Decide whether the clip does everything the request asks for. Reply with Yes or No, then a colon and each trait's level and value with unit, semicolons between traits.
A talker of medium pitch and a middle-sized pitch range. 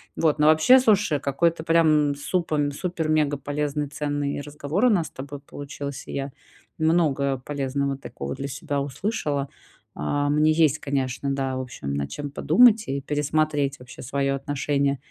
No: medium, 145 Hz; narrow, 2.1 semitones